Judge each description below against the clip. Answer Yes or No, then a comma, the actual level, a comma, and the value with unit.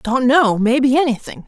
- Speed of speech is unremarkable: Yes, average, 165 wpm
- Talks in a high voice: Yes, very high, 255 Hz